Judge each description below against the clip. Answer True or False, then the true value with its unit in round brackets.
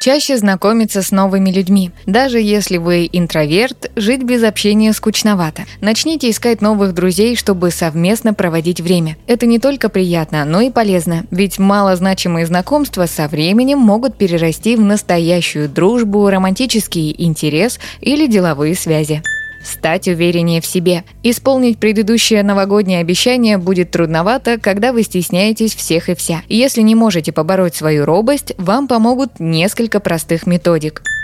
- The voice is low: False (195 Hz)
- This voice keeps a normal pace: True (135 wpm)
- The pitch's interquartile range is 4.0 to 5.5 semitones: True (4.7 semitones)